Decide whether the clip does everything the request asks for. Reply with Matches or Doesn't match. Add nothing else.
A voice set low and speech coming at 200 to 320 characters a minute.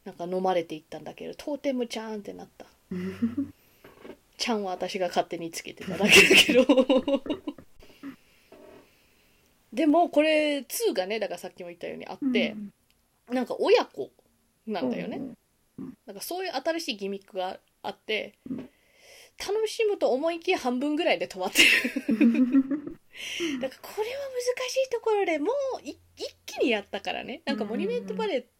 Doesn't match